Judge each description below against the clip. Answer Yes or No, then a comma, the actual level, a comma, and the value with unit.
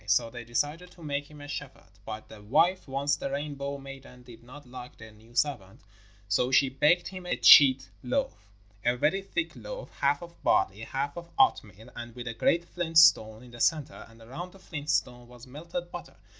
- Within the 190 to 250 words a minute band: Yes, average, 200 wpm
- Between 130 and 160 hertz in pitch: Yes, low, 135 Hz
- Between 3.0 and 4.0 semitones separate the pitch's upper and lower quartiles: No, average, 4.9 semitones